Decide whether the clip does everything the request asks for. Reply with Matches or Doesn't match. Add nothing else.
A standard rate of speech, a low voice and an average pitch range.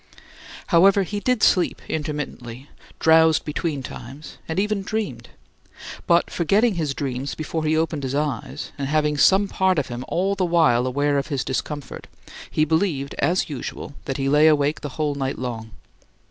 Doesn't match